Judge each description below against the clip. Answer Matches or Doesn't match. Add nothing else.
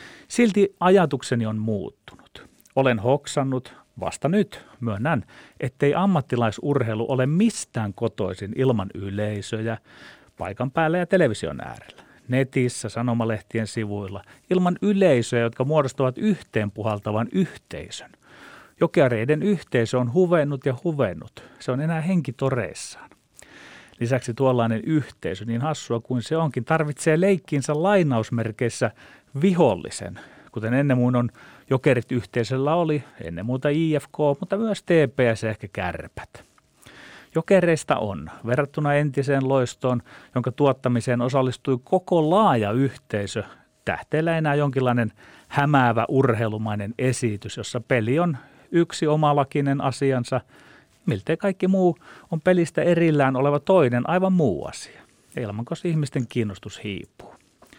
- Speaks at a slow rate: Doesn't match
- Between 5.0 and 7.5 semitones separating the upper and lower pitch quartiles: Matches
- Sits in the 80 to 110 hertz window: Doesn't match